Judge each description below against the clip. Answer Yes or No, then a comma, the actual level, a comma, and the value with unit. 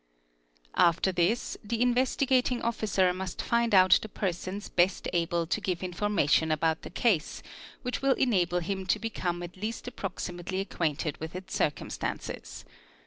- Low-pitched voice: No, medium, 185 Hz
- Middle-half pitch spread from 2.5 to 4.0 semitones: No, average, 4.4 semitones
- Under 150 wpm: Yes, average, 140 wpm